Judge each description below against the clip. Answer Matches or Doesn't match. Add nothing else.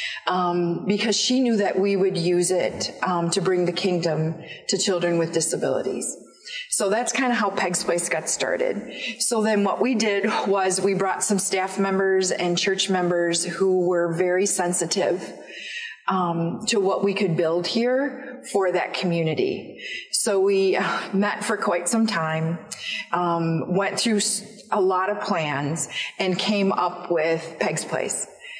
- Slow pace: Doesn't match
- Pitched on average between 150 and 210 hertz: Matches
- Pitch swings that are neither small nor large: Matches